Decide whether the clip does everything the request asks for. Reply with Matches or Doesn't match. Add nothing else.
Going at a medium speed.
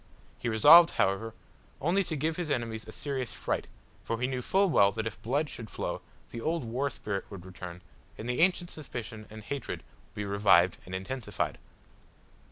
Matches